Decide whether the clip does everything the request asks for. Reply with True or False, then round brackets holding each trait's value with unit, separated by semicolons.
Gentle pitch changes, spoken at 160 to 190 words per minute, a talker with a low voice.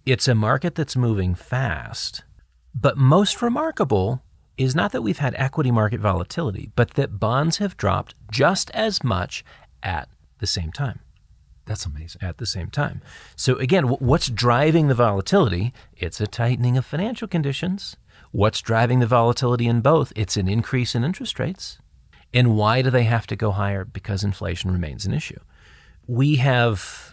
False (4.8 semitones; 165 wpm; 120 Hz)